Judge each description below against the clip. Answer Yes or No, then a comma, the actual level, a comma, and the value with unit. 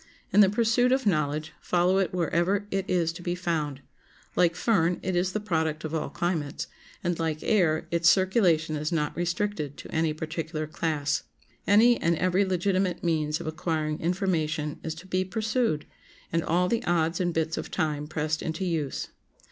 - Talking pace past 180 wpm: No, average, 175 wpm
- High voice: No, medium, 170 Hz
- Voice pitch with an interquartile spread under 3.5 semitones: Yes, average, 3.1 semitones